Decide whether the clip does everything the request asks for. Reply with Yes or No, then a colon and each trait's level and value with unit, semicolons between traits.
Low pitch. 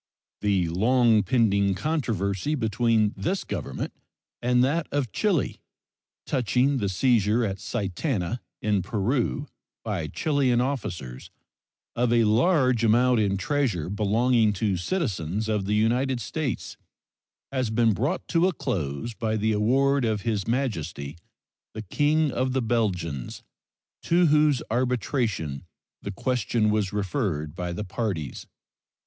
Yes: low, 115 Hz